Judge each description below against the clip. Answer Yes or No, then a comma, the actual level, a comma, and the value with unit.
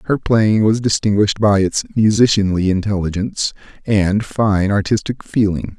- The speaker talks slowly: Yes, slow, 125 wpm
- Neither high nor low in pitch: No, low, 105 Hz